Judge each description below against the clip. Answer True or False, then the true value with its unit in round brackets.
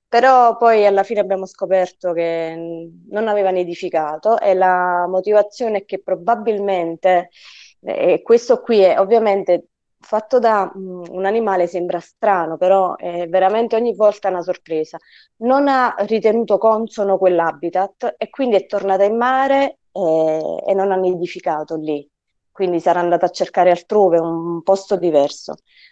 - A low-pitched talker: False (190 Hz)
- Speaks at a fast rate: False (140 wpm)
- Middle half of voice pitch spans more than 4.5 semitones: False (3.6 semitones)